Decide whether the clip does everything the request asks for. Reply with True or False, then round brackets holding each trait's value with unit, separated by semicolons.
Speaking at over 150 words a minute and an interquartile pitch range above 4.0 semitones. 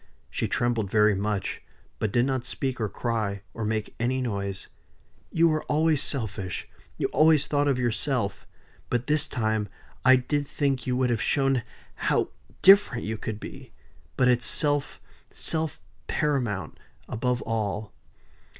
False (145 wpm; 4.4 semitones)